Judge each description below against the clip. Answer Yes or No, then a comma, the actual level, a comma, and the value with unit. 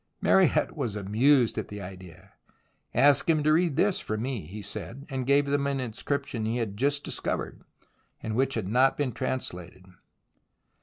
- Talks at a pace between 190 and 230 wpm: No, average, 175 wpm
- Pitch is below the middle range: Yes, low, 125 Hz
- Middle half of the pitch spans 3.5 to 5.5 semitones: Yes, average, 4.9 semitones